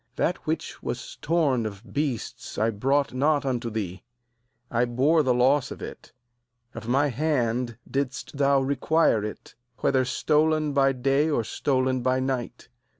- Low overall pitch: Yes, low, 130 Hz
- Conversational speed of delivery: Yes, average, 150 wpm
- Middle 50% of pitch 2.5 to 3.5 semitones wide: Yes, average, 3.1 semitones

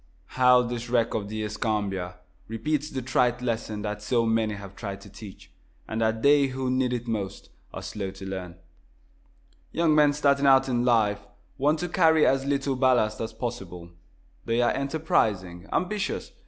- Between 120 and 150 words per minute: No, average, 170 wpm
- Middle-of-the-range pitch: No, low, 115 Hz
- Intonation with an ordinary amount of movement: Yes, average, 4.3 semitones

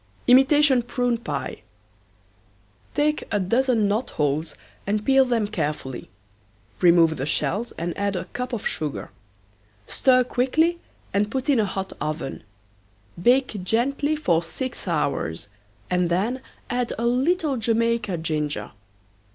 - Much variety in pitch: Yes, wide, 6.9 semitones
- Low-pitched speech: No, high, 225 Hz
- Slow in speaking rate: Yes, slow, 125 wpm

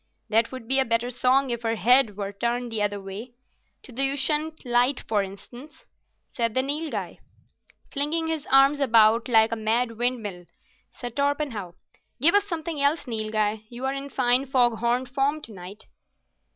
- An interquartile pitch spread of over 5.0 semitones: No, average, 3.7 semitones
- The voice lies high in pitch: Yes, high, 245 Hz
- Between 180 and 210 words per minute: No, average, 160 wpm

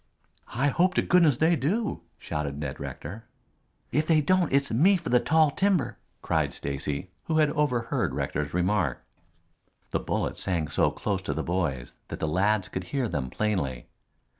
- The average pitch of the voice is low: Yes, low, 110 Hz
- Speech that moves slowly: No, average, 165 wpm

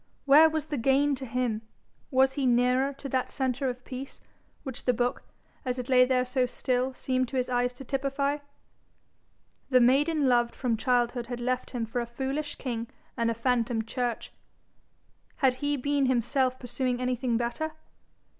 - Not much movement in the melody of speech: Yes, narrow, 1.8 semitones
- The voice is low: No, very high, 255 Hz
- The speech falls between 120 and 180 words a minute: Yes, average, 170 wpm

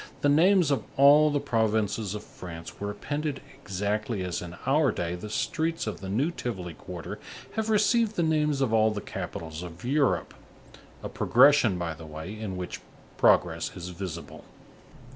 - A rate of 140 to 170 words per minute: Yes, average, 165 wpm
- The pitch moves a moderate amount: No, wide, 8.2 semitones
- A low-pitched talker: Yes, low, 110 Hz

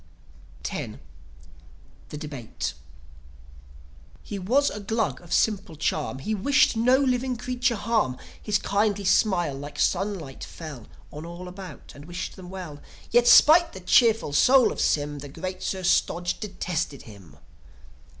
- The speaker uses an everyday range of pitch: No, wide, 6.8 semitones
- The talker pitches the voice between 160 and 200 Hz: Yes, medium, 185 Hz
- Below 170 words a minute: Yes, average, 140 wpm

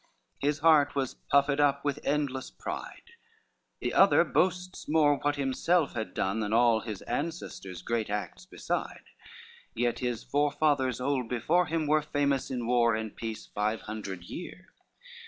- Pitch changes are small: No, average, 4.5 semitones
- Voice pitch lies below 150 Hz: Yes, low, 135 Hz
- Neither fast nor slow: Yes, average, 150 wpm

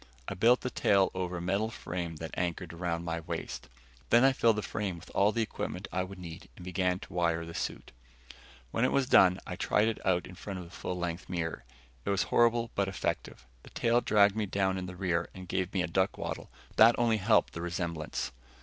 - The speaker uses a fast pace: Yes, fast, 230 wpm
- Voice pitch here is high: No, very low, 95 Hz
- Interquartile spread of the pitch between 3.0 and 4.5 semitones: Yes, average, 3.3 semitones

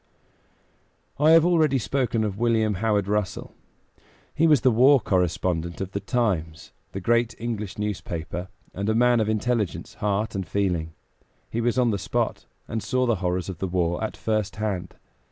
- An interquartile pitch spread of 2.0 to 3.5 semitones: No, average, 4.2 semitones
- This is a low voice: Yes, low, 105 Hz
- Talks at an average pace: Yes, average, 170 wpm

